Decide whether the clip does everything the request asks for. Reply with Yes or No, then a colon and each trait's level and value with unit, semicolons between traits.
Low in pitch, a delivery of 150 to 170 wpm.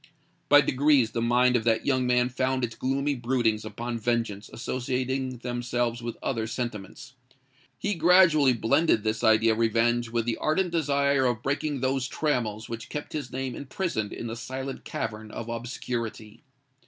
Yes: low, 125 Hz; average, 160 wpm